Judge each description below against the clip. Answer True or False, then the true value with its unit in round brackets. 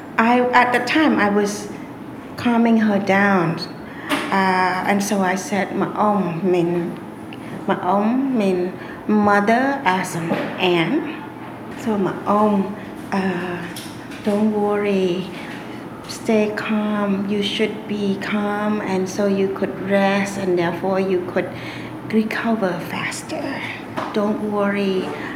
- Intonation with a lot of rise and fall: False (2.4 semitones)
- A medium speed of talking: False (115 wpm)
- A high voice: True (200 Hz)